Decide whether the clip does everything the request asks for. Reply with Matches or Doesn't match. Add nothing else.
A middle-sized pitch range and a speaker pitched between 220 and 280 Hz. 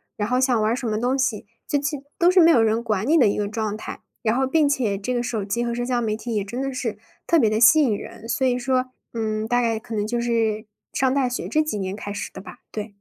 Matches